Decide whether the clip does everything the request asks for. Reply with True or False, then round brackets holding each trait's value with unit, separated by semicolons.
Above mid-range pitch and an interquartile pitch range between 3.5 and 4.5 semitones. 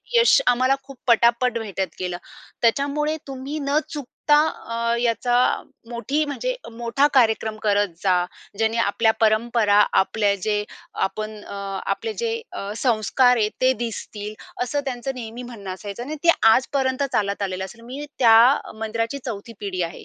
True (235 Hz; 3.8 semitones)